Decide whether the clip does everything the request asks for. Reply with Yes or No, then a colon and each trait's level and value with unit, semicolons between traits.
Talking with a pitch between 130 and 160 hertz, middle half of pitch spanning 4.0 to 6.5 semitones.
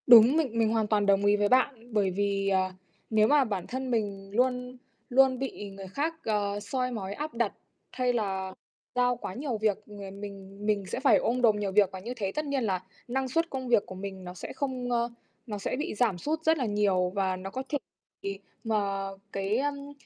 No: high, 215 Hz; average, 4.3 semitones